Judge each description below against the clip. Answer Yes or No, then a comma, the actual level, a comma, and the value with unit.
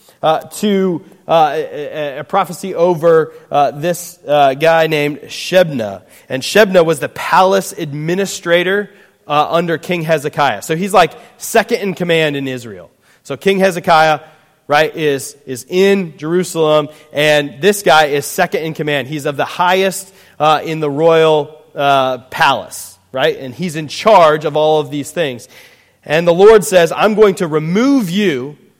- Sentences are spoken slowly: No, average, 155 wpm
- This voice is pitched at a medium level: Yes, medium, 160 Hz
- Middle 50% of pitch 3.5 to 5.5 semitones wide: Yes, average, 3.9 semitones